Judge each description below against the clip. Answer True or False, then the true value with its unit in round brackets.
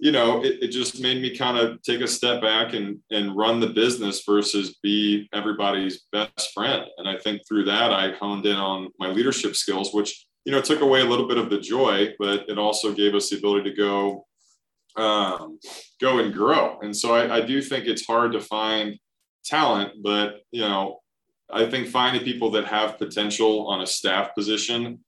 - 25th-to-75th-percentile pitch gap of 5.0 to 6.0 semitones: False (2.5 semitones)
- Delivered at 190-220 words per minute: True (200 wpm)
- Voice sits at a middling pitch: False (105 Hz)